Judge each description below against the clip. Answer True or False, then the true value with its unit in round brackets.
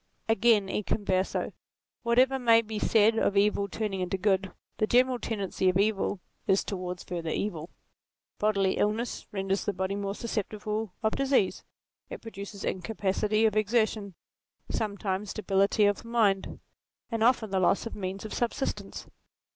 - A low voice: False (205 Hz)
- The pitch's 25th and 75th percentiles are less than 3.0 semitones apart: True (2.5 semitones)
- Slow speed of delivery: False (145 wpm)